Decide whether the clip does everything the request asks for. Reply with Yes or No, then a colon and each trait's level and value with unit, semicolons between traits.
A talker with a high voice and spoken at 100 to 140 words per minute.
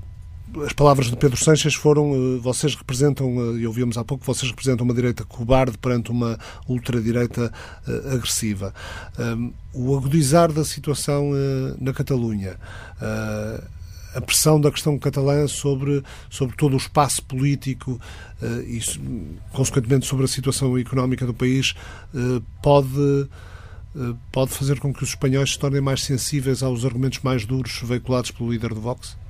No: low, 125 Hz; average, 135 wpm